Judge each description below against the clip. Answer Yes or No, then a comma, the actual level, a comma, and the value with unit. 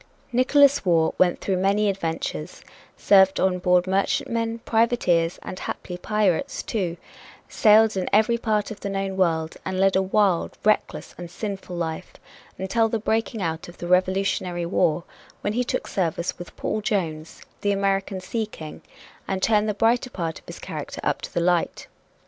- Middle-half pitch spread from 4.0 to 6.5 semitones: No, average, 3.3 semitones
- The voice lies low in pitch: No, high, 195 Hz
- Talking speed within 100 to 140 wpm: No, average, 165 wpm